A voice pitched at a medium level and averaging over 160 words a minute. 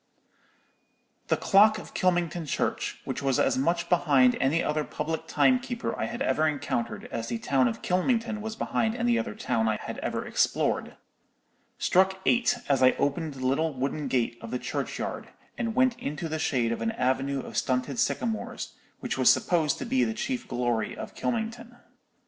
Yes: medium, 160 Hz; average, 175 wpm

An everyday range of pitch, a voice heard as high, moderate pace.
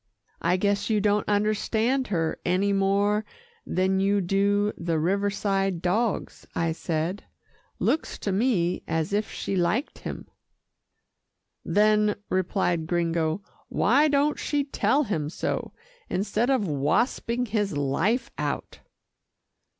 No: average, 3.4 semitones; high, 200 Hz; slow, 120 wpm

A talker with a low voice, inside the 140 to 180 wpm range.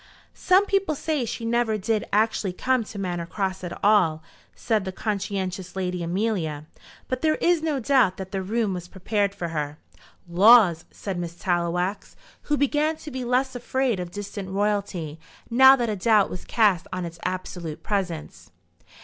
No: high, 200 Hz; average, 165 wpm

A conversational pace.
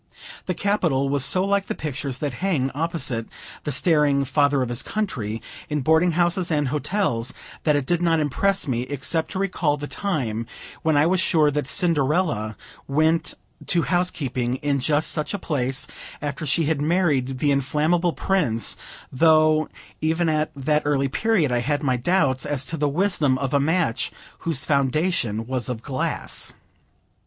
Yes: average, 165 wpm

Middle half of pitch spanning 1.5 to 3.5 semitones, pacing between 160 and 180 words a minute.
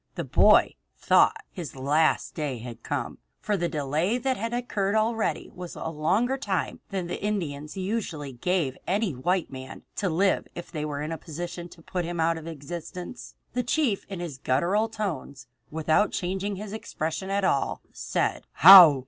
No: average, 4.7 semitones; average, 175 wpm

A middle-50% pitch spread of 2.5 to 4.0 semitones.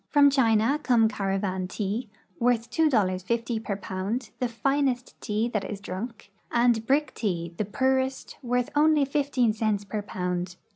No: average, 4.5 semitones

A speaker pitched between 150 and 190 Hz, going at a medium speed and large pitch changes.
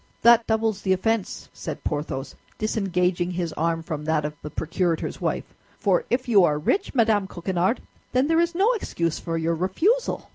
Yes: medium, 185 Hz; average, 175 wpm; wide, 6.0 semitones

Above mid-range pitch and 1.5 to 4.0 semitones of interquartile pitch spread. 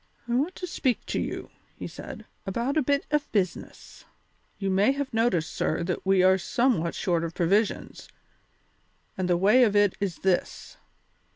No: high, 200 Hz; wide, 5.6 semitones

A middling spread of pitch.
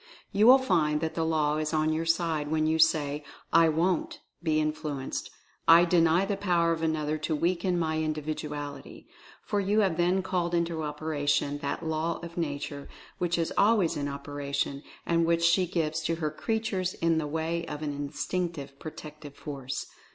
No: narrow, 2.2 semitones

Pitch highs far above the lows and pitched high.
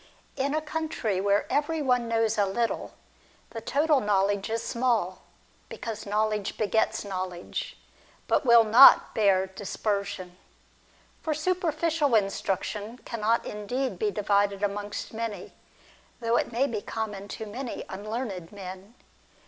No: average, 3.7 semitones; high, 220 Hz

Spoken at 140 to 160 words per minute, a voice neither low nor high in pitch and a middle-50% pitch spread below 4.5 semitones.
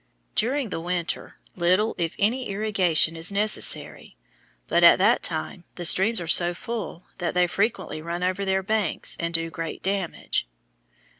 Yes: average, 155 wpm; medium, 180 Hz; average, 3.6 semitones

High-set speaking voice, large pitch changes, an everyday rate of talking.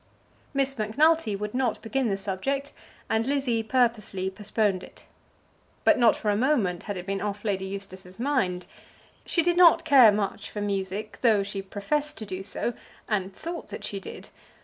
No: high, 210 Hz; average, 5.0 semitones; average, 170 wpm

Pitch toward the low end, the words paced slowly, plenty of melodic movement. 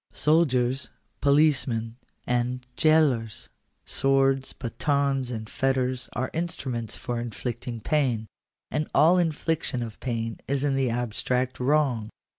No: low, 130 Hz; slow, 115 wpm; average, 2.9 semitones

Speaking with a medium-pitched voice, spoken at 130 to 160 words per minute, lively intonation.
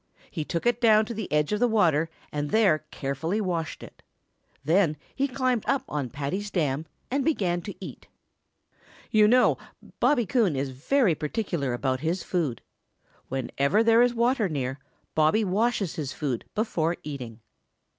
Yes: medium, 175 Hz; average, 155 wpm; wide, 7.1 semitones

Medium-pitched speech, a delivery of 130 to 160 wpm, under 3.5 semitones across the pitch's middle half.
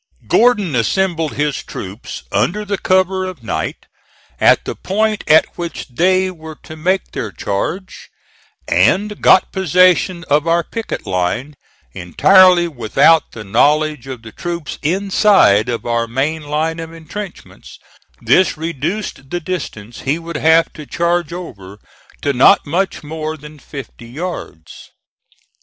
No: medium, 160 Hz; slow, 135 wpm; wide, 5.4 semitones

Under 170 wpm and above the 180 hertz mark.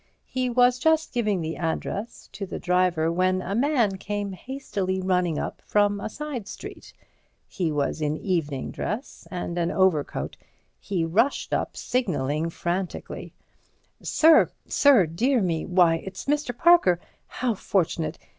Yes: slow, 135 wpm; high, 190 Hz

